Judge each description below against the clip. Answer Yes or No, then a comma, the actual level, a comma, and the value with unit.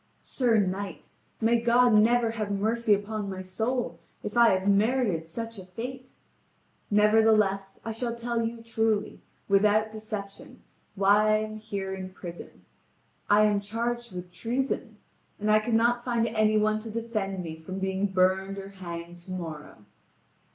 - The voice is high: Yes, high, 215 Hz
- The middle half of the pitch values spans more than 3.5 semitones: No, average, 3.0 semitones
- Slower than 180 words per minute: Yes, average, 150 wpm